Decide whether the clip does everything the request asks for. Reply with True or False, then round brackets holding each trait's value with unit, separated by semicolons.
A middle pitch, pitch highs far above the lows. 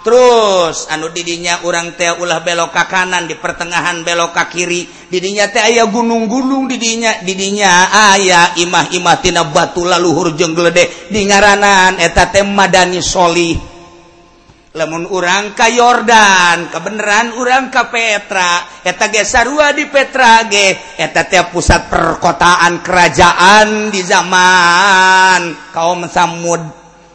False (180 Hz; 3.1 semitones)